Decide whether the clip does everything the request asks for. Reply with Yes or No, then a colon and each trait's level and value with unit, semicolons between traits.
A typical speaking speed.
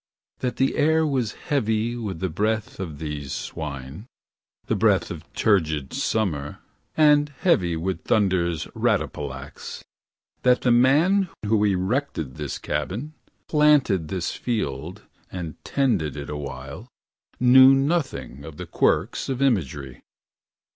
No: slow, 120 wpm